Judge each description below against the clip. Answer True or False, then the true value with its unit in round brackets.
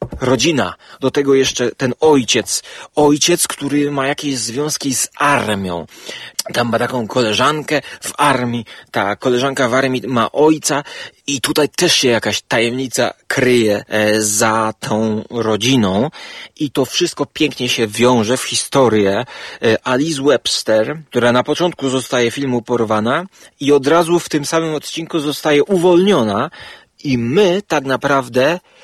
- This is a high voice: False (135 Hz)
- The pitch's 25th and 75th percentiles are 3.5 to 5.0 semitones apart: True (4.1 semitones)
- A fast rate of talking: False (135 wpm)